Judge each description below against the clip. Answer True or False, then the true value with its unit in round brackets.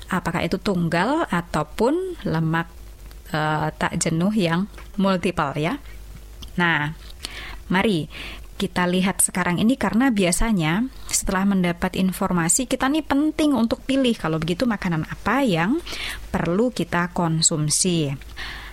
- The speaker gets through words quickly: False (110 wpm)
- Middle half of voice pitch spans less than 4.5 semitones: False (4.9 semitones)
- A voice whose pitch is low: False (185 Hz)